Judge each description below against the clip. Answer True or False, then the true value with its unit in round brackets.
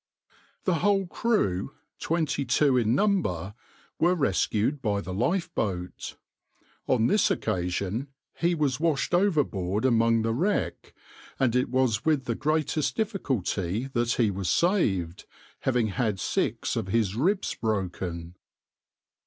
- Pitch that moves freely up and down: True (8.0 semitones)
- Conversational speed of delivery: False (125 wpm)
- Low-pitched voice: True (120 Hz)